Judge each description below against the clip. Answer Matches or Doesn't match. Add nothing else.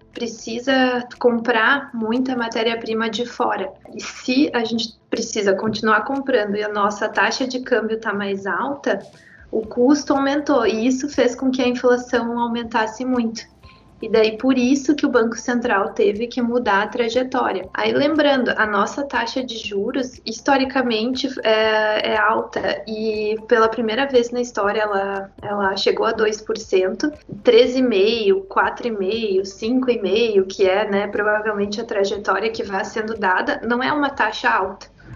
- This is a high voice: Matches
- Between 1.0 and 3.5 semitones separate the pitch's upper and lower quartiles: Matches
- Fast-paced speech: Doesn't match